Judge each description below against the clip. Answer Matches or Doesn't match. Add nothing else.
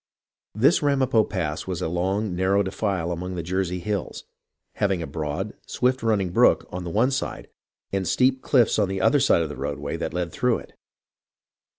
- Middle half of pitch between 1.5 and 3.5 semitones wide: Doesn't match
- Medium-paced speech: Matches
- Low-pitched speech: Matches